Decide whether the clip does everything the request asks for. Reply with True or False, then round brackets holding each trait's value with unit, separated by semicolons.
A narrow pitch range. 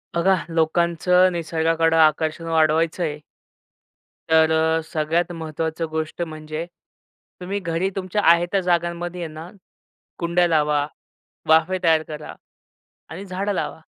True (1.7 semitones)